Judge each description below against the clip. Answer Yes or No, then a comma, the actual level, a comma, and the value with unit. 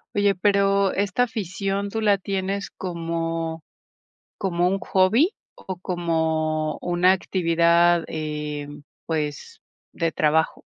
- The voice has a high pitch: No, medium, 175 Hz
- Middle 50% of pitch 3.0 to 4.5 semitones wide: Yes, average, 3.4 semitones